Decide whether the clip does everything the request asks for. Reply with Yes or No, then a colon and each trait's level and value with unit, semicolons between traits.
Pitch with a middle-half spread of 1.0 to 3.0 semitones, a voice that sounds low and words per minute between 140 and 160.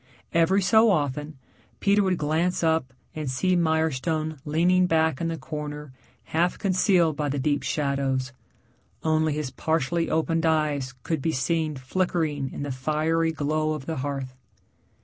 No: narrow, 2.5 semitones; medium, 155 Hz; average, 150 wpm